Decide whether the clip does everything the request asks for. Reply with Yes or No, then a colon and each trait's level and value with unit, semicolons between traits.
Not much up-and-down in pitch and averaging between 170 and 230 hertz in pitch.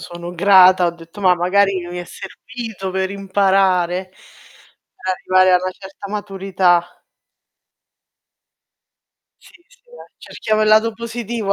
Yes: narrow, 2.2 semitones; high, 190 Hz